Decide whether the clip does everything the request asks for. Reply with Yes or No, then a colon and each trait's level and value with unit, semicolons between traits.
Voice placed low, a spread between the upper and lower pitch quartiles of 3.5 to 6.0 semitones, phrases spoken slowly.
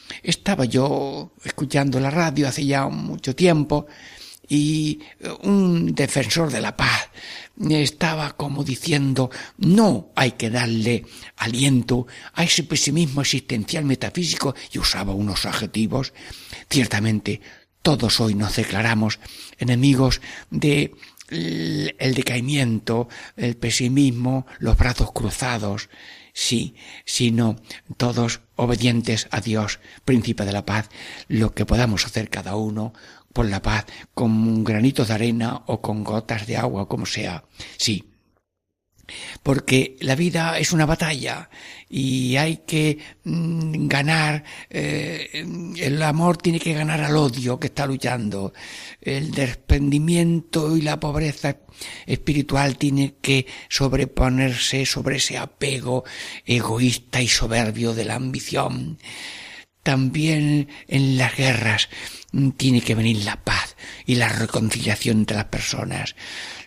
Yes: low, 130 Hz; average, 4.5 semitones; slow, 120 wpm